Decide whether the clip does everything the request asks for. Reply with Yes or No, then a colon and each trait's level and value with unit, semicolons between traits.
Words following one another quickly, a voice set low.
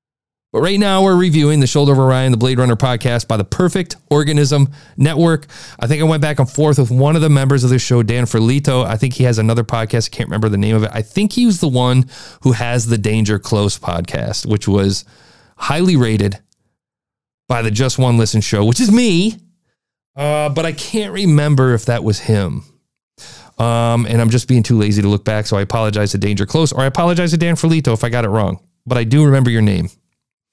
Yes: fast, 225 wpm; low, 125 Hz